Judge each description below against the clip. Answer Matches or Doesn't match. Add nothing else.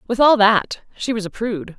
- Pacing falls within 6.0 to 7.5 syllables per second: Doesn't match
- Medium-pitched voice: Doesn't match